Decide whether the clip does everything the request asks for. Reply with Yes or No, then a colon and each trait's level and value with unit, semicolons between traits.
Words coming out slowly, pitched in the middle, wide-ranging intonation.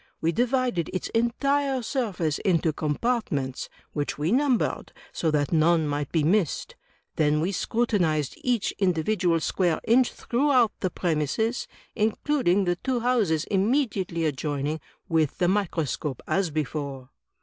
Yes: slow, 125 wpm; medium, 175 Hz; wide, 7.1 semitones